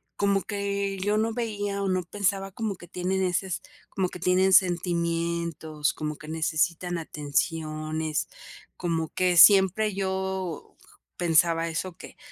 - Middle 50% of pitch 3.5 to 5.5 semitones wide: No, average, 2.9 semitones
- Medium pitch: Yes, medium, 180 Hz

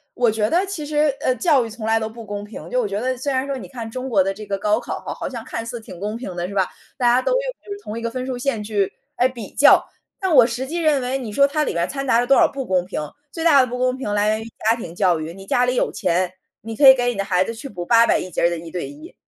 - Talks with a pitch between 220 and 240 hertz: Yes, high, 235 Hz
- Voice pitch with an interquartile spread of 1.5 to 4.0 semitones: No, average, 4.4 semitones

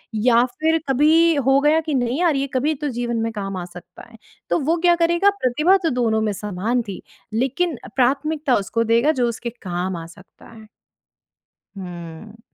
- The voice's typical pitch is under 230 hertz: No, high, 245 Hz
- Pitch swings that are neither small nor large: No, wide, 6.0 semitones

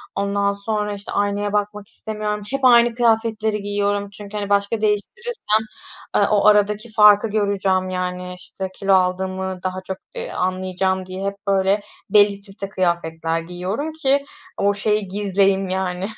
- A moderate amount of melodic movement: No, narrow, 1.9 semitones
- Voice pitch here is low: No, high, 200 Hz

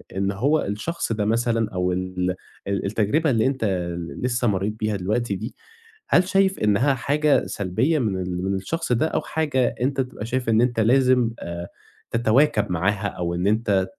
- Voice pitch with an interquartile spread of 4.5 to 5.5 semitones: Yes, average, 5.1 semitones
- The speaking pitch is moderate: No, low, 110 Hz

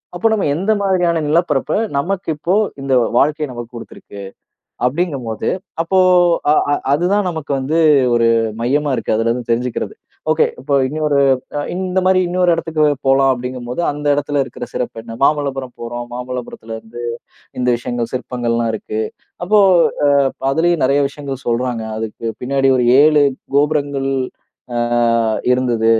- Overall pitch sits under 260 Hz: Yes, low, 135 Hz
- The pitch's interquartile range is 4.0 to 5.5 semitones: Yes, average, 4.3 semitones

